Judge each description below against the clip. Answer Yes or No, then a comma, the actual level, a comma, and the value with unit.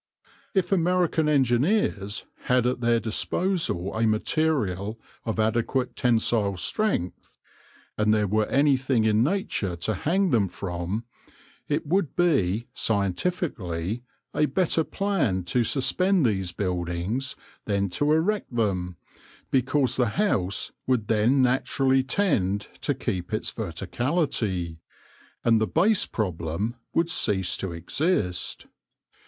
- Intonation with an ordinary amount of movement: No, wide, 7.4 semitones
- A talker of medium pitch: No, low, 115 Hz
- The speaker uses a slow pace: Yes, slow, 115 wpm